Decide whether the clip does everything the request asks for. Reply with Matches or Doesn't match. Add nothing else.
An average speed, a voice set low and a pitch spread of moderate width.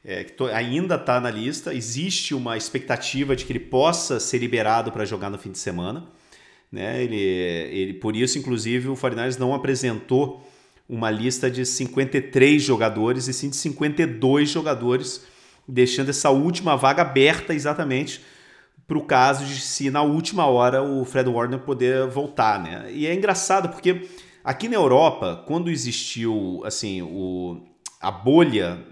Matches